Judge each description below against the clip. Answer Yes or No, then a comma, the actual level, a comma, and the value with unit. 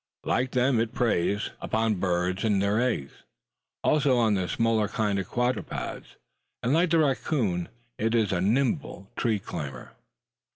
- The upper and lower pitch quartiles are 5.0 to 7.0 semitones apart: No, average, 4.3 semitones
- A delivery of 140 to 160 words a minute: Yes, average, 155 wpm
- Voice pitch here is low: Yes, low, 110 Hz